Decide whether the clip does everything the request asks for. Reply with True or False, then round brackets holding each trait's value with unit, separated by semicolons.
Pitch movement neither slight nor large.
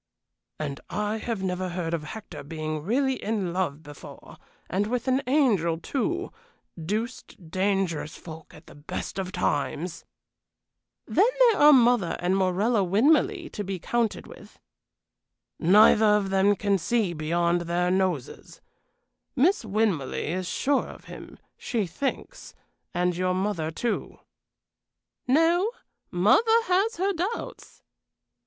False (6.2 semitones)